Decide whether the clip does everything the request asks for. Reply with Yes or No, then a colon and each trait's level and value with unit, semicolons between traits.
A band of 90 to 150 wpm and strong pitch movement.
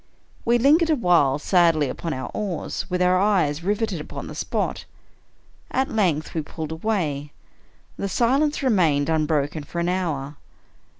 Yes: average, 140 wpm; wide, 5.8 semitones